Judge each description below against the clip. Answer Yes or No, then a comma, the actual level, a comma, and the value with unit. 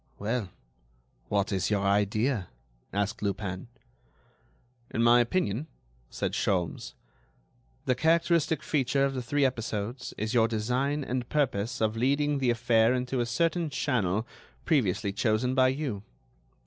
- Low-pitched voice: Yes, low, 120 Hz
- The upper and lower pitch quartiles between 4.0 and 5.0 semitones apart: Yes, average, 4.5 semitones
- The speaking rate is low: Yes, slow, 130 wpm